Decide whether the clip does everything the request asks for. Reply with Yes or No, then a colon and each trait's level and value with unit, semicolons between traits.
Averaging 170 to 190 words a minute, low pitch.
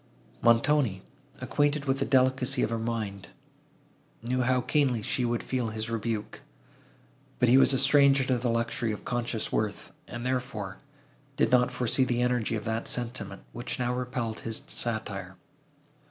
No: average, 155 wpm; low, 120 Hz